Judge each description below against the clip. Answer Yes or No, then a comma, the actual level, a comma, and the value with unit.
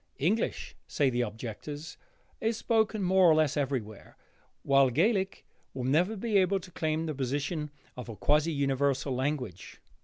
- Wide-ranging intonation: Yes, wide, 5.7 semitones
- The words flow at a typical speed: Yes, average, 150 wpm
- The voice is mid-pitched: Yes, medium, 150 Hz